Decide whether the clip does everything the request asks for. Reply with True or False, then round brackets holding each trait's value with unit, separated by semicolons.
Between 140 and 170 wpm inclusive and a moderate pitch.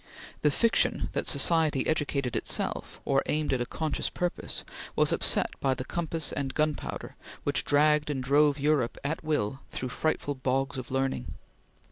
True (155 wpm; 145 Hz)